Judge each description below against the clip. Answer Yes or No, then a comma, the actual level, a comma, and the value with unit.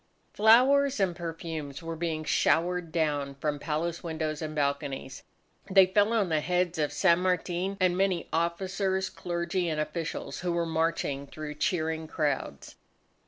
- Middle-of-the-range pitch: Yes, medium, 170 Hz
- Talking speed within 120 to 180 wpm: Yes, average, 145 wpm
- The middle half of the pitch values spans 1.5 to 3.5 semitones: Yes, average, 3.0 semitones